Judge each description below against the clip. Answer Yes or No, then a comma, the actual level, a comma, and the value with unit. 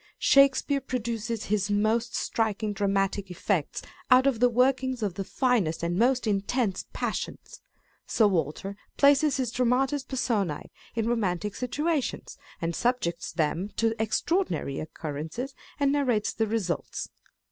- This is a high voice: Yes, high, 225 Hz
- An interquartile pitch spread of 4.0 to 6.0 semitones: Yes, average, 4.7 semitones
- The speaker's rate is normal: No, slow, 125 wpm